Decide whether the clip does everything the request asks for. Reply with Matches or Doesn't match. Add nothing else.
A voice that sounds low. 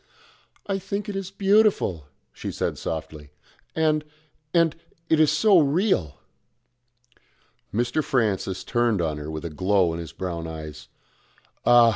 Matches